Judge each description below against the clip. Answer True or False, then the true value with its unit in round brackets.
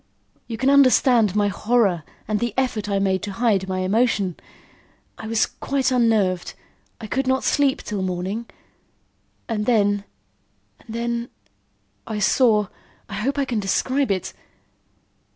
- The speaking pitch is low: False (220 Hz)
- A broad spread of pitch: False (3.7 semitones)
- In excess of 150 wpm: False (140 wpm)